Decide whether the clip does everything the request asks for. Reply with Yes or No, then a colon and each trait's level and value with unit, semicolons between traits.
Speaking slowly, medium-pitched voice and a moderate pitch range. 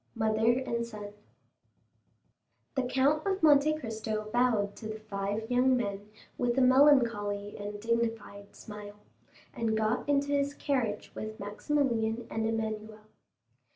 No: slow, 125 wpm; high, 225 Hz; average, 3.4 semitones